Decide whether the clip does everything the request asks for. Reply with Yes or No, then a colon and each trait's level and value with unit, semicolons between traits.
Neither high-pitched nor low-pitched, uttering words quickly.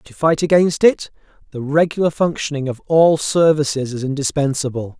No: medium, 150 Hz; average, 145 wpm